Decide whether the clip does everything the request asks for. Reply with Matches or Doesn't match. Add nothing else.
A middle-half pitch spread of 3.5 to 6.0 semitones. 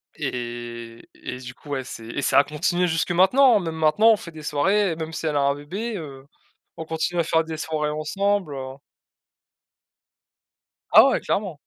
Matches